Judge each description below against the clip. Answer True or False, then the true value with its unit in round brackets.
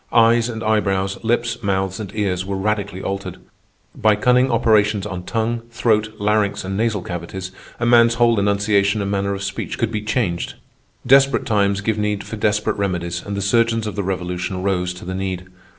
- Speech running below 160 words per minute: False (180 wpm)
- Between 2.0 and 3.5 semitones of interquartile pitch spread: True (2.7 semitones)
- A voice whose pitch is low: True (105 Hz)